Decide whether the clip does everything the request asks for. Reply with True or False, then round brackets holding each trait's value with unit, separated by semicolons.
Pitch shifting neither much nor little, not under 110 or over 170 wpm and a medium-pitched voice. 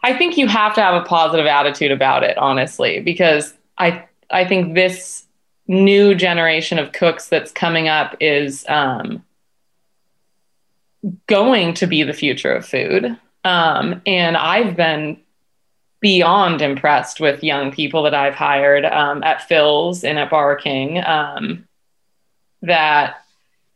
True (3.8 semitones; 135 wpm; 165 Hz)